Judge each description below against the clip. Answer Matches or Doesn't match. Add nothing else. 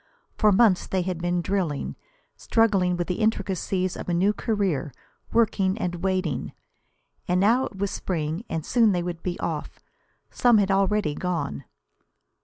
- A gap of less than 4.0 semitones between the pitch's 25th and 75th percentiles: Matches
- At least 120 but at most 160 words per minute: Matches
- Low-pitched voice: Doesn't match